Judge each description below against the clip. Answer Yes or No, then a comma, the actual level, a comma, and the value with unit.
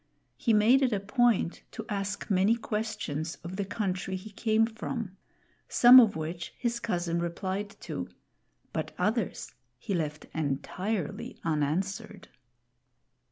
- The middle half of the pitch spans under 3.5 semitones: No, average, 4.3 semitones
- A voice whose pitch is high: Yes, high, 195 Hz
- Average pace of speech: No, slow, 125 wpm